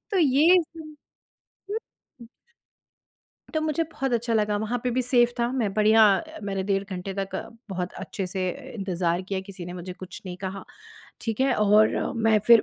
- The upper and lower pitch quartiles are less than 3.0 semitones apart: No, average, 4.5 semitones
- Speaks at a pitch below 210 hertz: No, high, 215 Hz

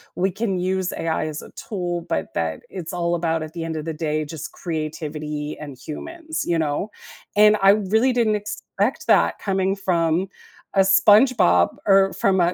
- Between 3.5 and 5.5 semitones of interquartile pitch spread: Yes, average, 3.9 semitones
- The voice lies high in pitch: No, medium, 175 Hz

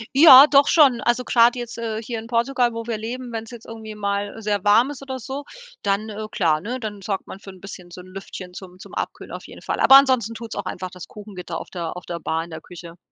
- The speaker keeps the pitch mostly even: No, average, 4.1 semitones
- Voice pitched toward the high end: Yes, high, 220 Hz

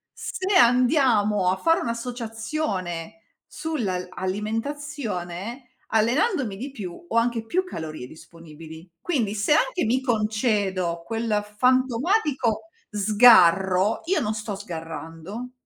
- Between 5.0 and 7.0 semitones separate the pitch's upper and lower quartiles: Yes, average, 5.3 semitones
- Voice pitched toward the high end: Yes, high, 220 Hz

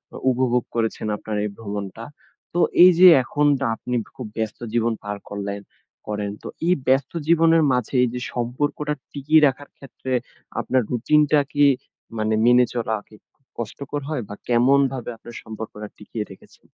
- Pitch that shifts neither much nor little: Yes, average, 4.6 semitones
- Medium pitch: No, low, 125 Hz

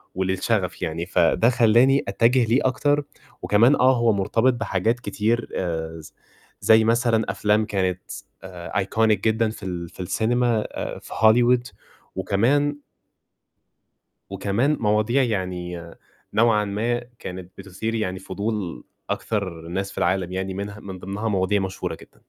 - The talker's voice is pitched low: Yes, low, 105 Hz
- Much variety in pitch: No, average, 3.8 semitones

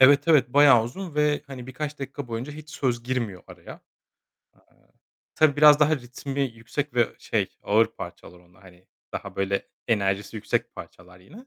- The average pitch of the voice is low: Yes, low, 130 Hz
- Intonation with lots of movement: No, average, 5.0 semitones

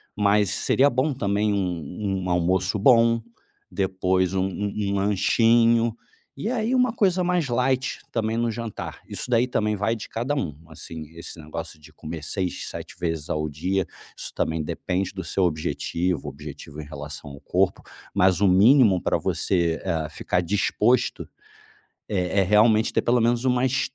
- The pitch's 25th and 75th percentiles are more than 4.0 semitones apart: Yes, average, 5.1 semitones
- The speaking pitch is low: Yes, low, 100 Hz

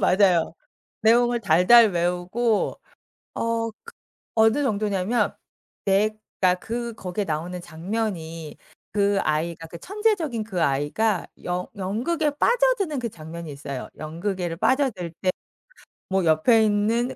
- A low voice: No, high, 200 Hz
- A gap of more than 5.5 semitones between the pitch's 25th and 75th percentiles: No, average, 5.2 semitones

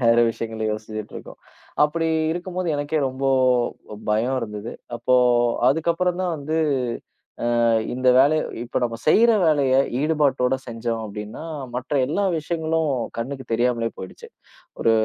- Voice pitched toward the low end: Yes, low, 130 Hz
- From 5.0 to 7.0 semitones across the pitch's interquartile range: Yes, wide, 5.5 semitones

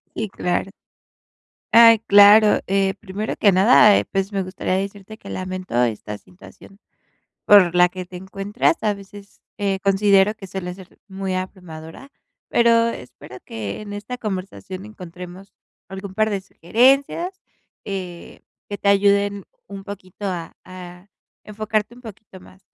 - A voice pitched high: Yes, high, 195 Hz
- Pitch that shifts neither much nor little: No, narrow, 2.1 semitones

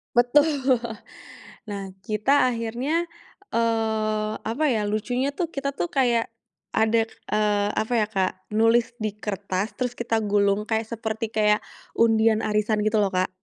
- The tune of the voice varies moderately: No, narrow, 2.1 semitones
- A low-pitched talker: No, high, 220 Hz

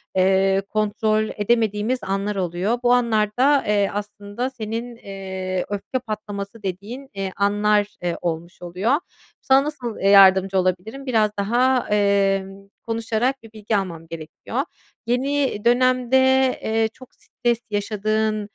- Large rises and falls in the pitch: No, average, 3.4 semitones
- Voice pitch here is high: Yes, high, 210 Hz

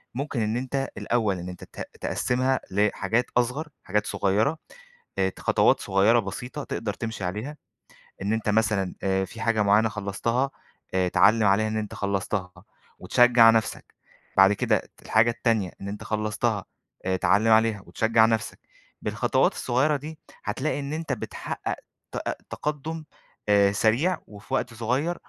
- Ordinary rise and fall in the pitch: Yes, average, 3.5 semitones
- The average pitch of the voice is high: No, low, 110 Hz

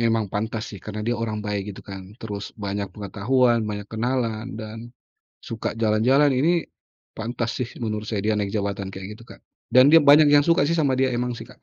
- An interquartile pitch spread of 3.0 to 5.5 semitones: Yes, average, 3.5 semitones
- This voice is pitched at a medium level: No, low, 110 Hz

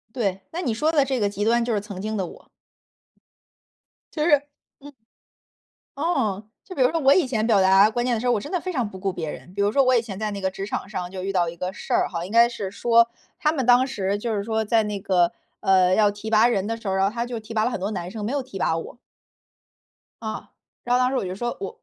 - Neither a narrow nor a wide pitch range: Yes, average, 4.2 semitones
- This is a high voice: Yes, high, 220 Hz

